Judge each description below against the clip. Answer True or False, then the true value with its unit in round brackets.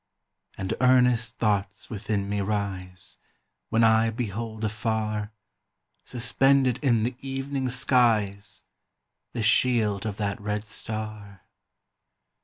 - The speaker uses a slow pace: True (100 wpm)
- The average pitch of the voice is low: True (110 Hz)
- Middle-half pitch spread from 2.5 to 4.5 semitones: True (2.9 semitones)